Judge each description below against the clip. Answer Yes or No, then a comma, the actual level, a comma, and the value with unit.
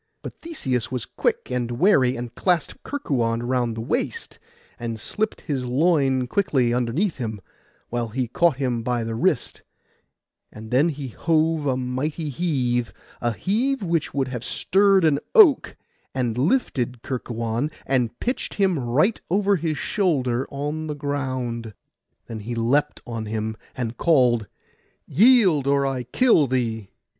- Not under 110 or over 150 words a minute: Yes, average, 145 wpm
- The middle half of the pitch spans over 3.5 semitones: Yes, average, 5.3 semitones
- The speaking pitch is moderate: No, low, 130 Hz